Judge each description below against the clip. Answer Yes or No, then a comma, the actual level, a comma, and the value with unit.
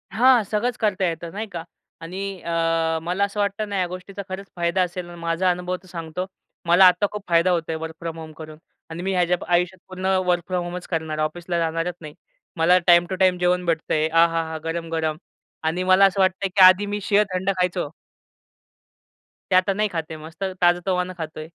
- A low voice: No, medium, 180 Hz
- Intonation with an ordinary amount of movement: No, narrow, 2.2 semitones